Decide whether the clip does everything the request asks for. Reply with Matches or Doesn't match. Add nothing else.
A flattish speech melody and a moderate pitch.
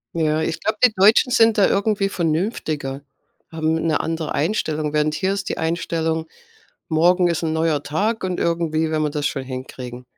Doesn't match